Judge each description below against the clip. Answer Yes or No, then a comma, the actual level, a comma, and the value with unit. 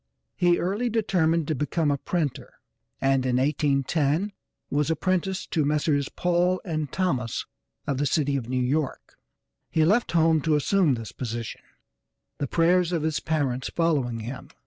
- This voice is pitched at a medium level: Yes, medium, 155 Hz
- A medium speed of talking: Yes, average, 150 wpm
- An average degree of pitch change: Yes, average, 4.2 semitones